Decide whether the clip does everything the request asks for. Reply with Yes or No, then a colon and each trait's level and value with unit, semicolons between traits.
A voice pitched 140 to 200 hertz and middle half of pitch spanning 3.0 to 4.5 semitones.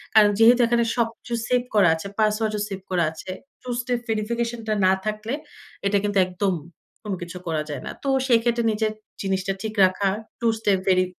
No: high, 210 Hz; average, 3.5 semitones